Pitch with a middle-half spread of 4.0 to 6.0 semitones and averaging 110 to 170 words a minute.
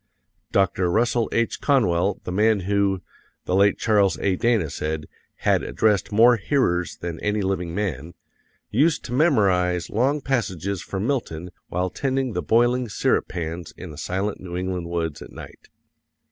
Yes: average, 4.6 semitones; average, 155 wpm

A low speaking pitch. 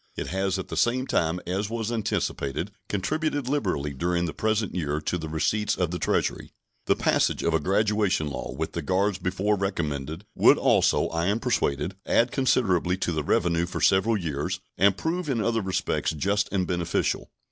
Yes: very low, 95 Hz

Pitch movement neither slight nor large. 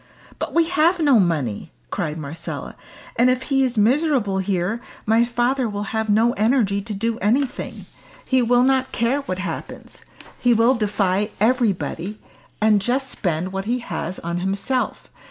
Yes: average, 4.6 semitones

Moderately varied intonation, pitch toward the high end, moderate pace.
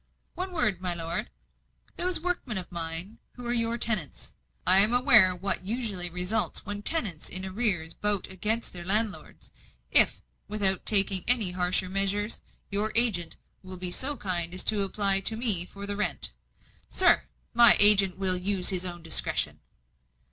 Yes: average, 3.5 semitones; high, 200 Hz; average, 160 wpm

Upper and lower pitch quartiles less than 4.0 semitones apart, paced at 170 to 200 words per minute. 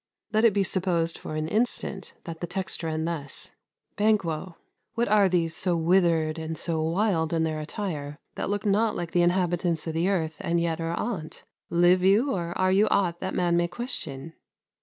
Yes: average, 3.1 semitones; average, 190 wpm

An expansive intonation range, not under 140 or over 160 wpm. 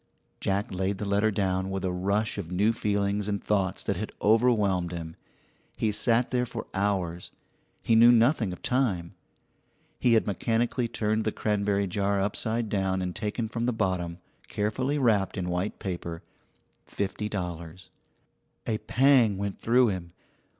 No: average, 3.1 semitones; average, 150 wpm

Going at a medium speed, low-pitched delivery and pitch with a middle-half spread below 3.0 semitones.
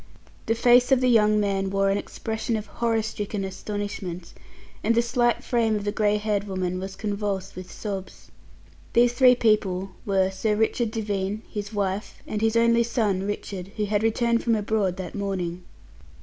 No: average, 175 wpm; high, 210 Hz; narrow, 2.5 semitones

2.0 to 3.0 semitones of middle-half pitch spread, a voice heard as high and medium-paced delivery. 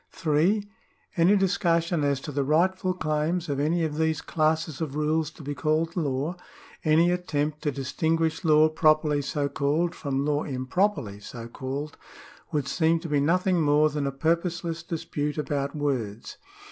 No: narrow, 2.6 semitones; medium, 155 Hz; average, 165 wpm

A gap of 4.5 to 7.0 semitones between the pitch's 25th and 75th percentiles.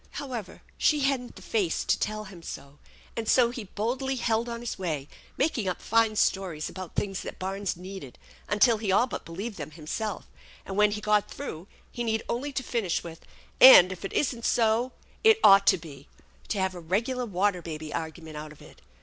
Yes: average, 5.0 semitones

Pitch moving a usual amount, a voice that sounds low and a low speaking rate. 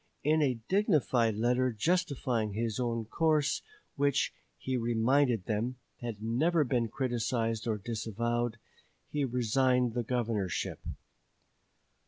Yes: average, 3.0 semitones; low, 120 Hz; slow, 110 wpm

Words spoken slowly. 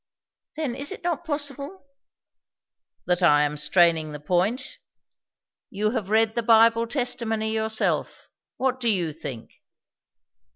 Yes: slow, 130 wpm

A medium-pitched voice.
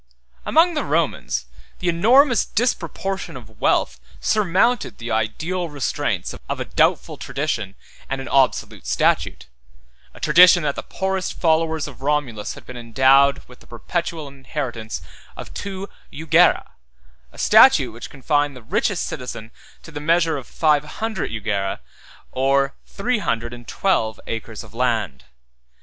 Yes: medium, 145 Hz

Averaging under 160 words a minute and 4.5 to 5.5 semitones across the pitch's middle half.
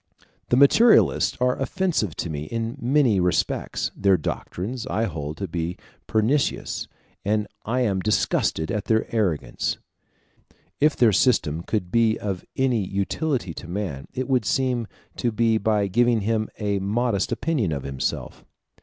Yes: average, 145 wpm; average, 5.0 semitones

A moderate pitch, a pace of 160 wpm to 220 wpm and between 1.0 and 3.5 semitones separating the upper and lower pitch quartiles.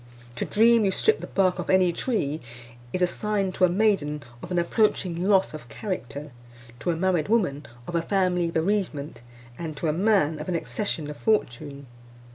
No: medium, 180 Hz; average, 190 wpm; average, 4.6 semitones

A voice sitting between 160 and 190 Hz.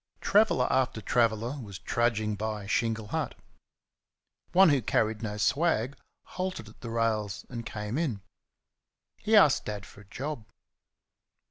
No: low, 115 Hz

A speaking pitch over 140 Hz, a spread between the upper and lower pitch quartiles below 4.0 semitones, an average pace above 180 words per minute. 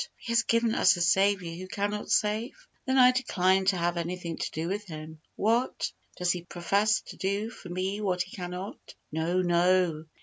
Yes: medium, 185 Hz; average, 3.2 semitones; average, 190 wpm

